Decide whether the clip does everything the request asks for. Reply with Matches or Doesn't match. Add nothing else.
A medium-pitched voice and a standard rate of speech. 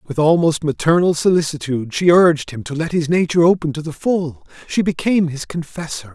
Matches